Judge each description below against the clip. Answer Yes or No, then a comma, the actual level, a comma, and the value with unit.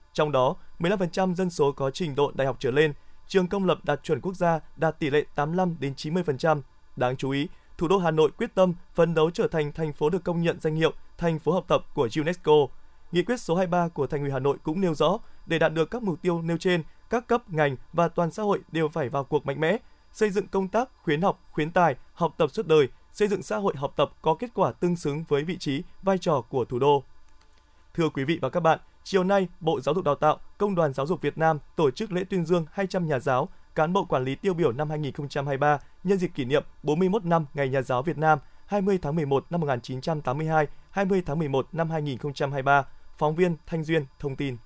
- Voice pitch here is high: No, medium, 160 Hz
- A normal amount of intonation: Yes, average, 4.1 semitones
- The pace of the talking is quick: No, average, 240 wpm